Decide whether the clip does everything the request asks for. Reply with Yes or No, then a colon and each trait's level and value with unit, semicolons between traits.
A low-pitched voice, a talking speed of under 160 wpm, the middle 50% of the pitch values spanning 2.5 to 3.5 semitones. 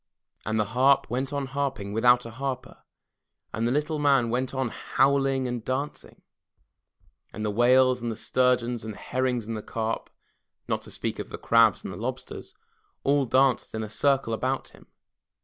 No: low, 125 Hz; average, 175 wpm; average, 2.9 semitones